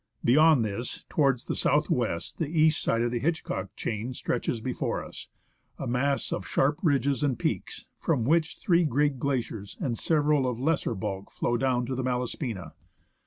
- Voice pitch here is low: Yes, low, 130 Hz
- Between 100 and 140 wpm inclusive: No, average, 170 wpm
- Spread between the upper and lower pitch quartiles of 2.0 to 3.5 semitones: No, average, 4.0 semitones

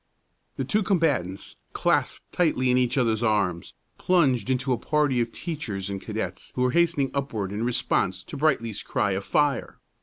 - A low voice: Yes, low, 125 Hz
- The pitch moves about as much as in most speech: No, wide, 6.0 semitones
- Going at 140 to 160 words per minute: No, average, 170 wpm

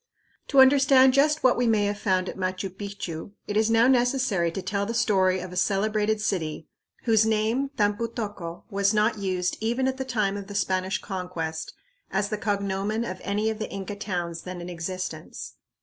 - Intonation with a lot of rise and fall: No, average, 3.2 semitones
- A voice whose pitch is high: Yes, high, 205 Hz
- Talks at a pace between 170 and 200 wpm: Yes, average, 190 wpm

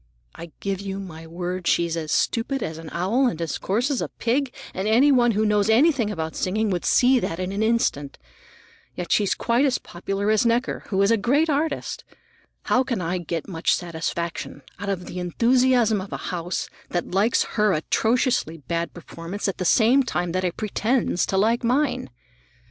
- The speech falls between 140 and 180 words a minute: No, average, 190 wpm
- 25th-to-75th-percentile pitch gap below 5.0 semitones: No, average, 5.3 semitones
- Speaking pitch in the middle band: No, high, 200 Hz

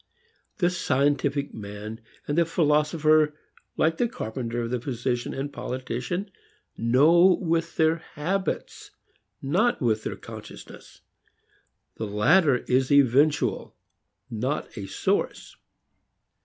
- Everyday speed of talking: No, slow, 100 wpm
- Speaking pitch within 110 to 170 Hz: Yes, medium, 140 Hz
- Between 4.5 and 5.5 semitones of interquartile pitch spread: Yes, average, 5.2 semitones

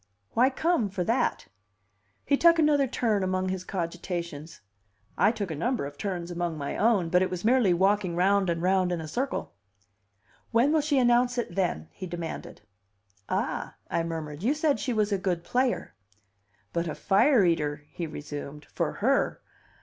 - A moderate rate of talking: Yes, average, 170 wpm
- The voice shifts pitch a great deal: Yes, wide, 6.1 semitones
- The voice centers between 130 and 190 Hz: Yes, medium, 185 Hz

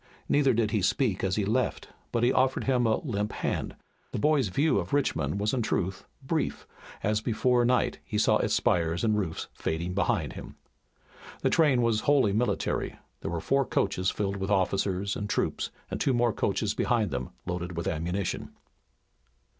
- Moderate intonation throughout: Yes, average, 4.7 semitones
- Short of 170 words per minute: No, average, 180 wpm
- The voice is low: Yes, low, 105 Hz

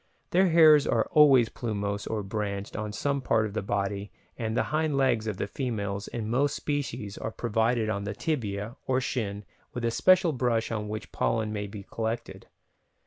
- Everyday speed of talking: Yes, average, 185 wpm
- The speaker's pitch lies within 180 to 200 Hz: No, low, 110 Hz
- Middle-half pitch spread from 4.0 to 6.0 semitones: Yes, average, 4.3 semitones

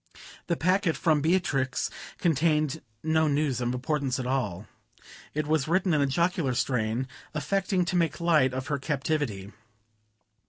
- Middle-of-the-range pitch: Yes, medium, 150 Hz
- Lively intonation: No, average, 4.1 semitones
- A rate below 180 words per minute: Yes, average, 145 wpm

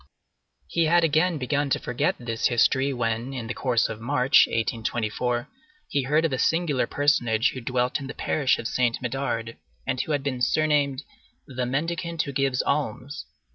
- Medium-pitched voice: No, low, 130 Hz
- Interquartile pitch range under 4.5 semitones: Yes, average, 3.3 semitones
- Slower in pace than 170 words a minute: No, average, 175 wpm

